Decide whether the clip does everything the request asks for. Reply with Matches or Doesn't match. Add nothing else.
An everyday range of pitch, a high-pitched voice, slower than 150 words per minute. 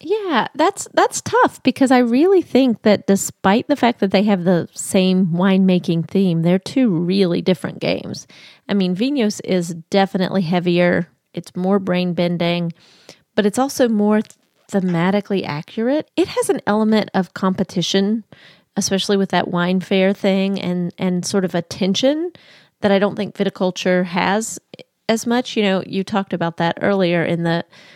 Doesn't match